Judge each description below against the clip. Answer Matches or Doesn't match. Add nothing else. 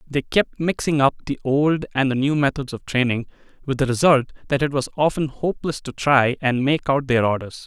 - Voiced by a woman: Doesn't match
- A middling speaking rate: Doesn't match